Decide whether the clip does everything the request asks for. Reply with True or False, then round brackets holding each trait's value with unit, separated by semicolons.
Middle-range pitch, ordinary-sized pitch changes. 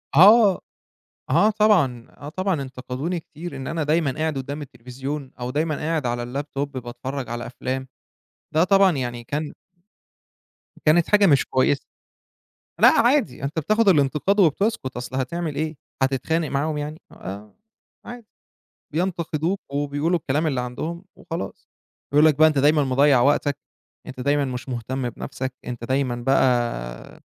True (145 Hz; 4.0 semitones)